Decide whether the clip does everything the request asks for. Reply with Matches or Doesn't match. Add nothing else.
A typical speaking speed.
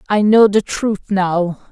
Matches